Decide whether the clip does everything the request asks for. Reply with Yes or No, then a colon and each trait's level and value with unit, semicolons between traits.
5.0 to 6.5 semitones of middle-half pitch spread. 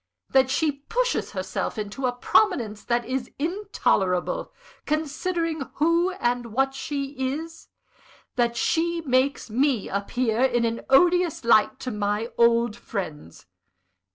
Yes: average, 5.3 semitones